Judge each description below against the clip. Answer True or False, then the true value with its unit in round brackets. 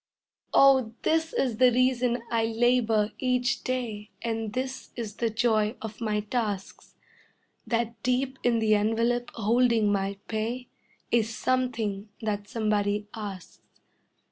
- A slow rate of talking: True (125 wpm)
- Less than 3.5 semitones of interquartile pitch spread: True (2.7 semitones)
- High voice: True (230 Hz)